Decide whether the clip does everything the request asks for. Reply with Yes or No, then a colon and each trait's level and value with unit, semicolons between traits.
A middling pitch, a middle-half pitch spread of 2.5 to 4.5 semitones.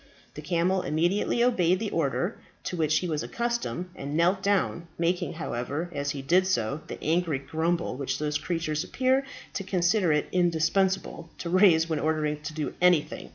Yes: medium, 170 Hz; average, 3.3 semitones